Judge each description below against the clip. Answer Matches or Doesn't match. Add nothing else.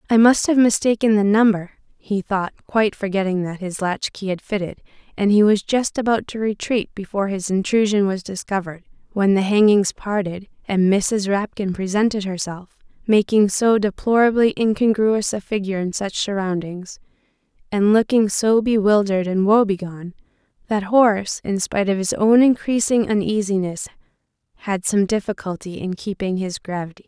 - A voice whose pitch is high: Matches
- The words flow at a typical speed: Matches